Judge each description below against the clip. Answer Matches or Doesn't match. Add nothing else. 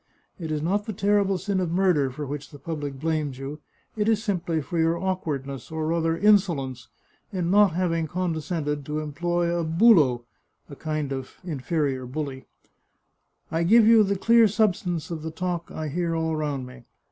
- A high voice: Doesn't match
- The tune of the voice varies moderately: Matches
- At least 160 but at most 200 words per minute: Matches